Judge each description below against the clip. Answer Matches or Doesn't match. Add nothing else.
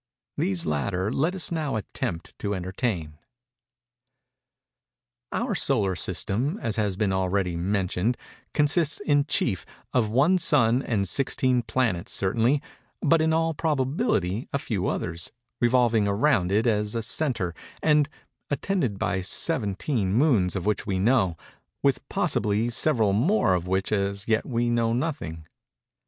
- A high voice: Doesn't match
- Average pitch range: Doesn't match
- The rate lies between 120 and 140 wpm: Matches